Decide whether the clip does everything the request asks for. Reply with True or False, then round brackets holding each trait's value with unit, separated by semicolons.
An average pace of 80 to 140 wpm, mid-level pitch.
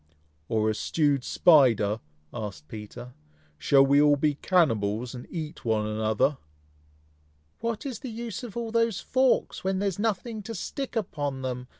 False (160 wpm; 145 Hz)